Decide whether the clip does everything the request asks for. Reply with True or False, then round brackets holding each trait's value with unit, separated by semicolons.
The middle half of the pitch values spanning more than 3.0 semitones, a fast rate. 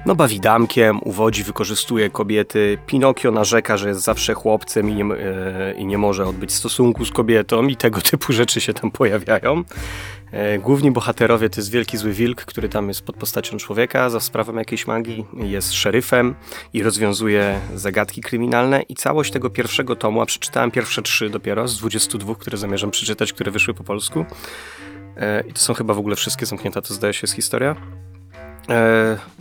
False (2.5 semitones; 175 wpm)